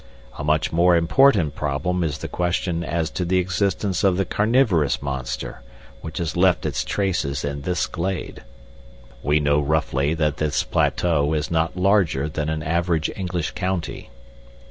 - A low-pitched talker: Yes, very low, 85 Hz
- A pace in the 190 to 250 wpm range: No, average, 155 wpm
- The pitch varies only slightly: No, average, 3.1 semitones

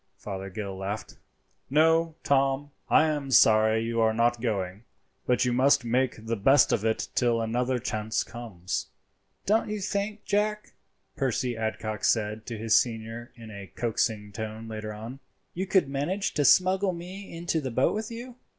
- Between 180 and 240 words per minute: No, average, 160 wpm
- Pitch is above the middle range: No, low, 120 Hz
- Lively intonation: Yes, wide, 6.0 semitones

